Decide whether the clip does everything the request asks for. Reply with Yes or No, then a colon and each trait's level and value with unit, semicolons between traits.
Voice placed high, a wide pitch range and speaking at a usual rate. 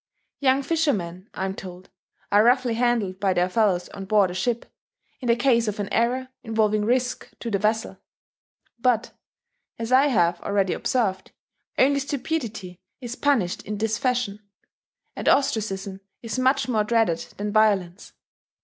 No: high, 220 Hz; average, 4.3 semitones; average, 150 wpm